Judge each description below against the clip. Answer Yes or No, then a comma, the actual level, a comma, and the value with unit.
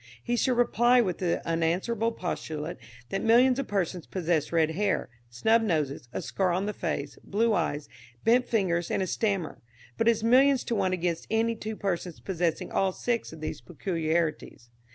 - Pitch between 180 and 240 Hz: Yes, high, 190 Hz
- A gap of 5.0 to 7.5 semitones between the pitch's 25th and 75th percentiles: Yes, wide, 5.5 semitones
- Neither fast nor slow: Yes, average, 175 wpm